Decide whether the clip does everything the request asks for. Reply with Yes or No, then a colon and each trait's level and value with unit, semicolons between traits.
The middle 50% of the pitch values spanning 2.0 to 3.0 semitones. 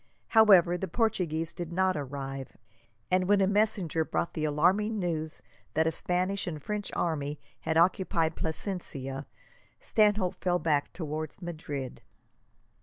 No: average, 3.7 semitones